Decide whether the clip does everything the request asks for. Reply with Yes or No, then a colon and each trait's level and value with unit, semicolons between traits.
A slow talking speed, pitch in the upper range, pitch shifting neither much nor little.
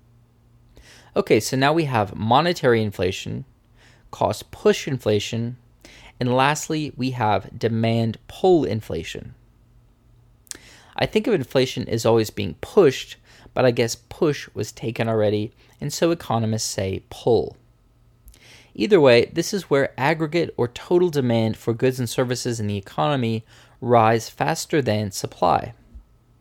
No: slow, 130 wpm; low, 120 Hz; average, 3.0 semitones